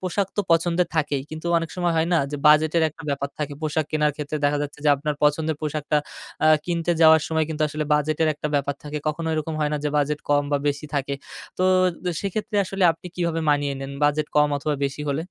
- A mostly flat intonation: Yes, narrow, 1.8 semitones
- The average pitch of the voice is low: No, medium, 150 Hz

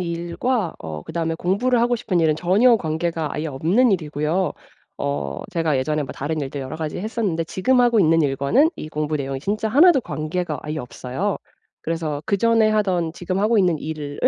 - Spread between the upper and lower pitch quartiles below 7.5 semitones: Yes, wide, 5.4 semitones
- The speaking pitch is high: No, medium, 165 Hz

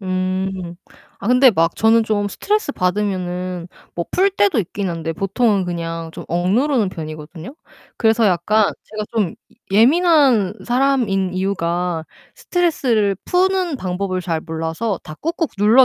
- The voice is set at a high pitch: Yes, high, 195 Hz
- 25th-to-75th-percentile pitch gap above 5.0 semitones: Yes, wide, 5.5 semitones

